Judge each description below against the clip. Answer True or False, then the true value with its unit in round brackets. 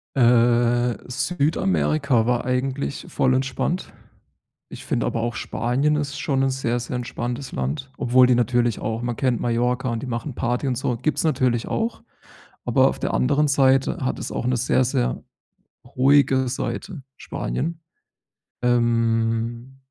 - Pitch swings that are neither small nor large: False (2.2 semitones)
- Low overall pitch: True (125 Hz)